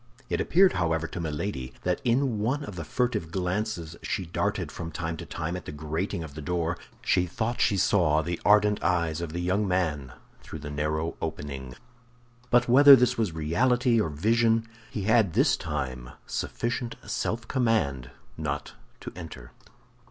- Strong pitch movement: Yes, wide, 6.2 semitones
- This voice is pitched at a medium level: No, very low, 85 Hz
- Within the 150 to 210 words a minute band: Yes, average, 165 wpm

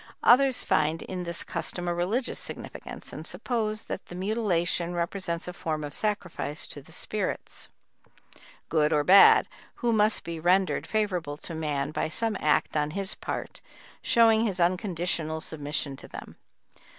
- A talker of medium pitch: Yes, medium, 175 Hz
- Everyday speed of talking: Yes, average, 150 wpm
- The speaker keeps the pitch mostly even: No, average, 4.8 semitones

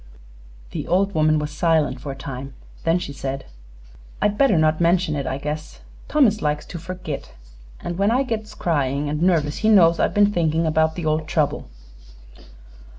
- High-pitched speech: No, medium, 160 Hz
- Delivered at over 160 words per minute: Yes, average, 175 wpm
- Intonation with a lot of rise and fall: No, average, 3.6 semitones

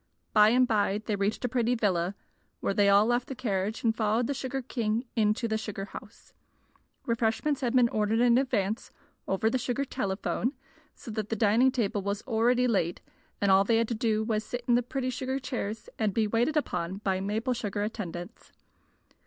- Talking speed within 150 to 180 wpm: No, average, 195 wpm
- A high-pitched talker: Yes, high, 225 Hz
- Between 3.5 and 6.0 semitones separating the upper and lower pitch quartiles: No, average, 3.1 semitones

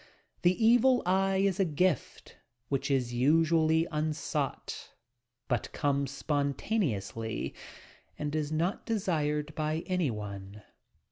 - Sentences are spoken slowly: Yes, slow, 110 wpm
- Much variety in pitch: No, average, 4.7 semitones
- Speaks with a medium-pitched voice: Yes, medium, 155 Hz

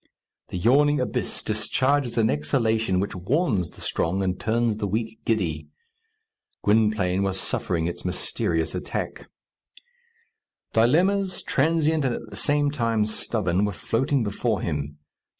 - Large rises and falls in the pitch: Yes, wide, 6.0 semitones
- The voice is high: No, low, 110 Hz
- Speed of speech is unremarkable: No, slow, 130 wpm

